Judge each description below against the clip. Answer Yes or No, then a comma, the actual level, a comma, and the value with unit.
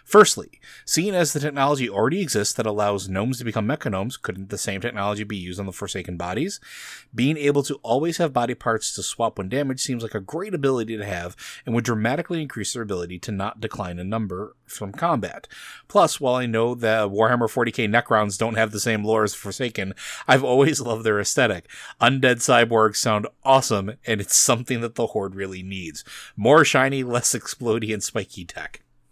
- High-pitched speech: No, low, 115 Hz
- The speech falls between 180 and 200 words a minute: Yes, average, 190 wpm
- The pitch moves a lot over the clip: No, average, 3.7 semitones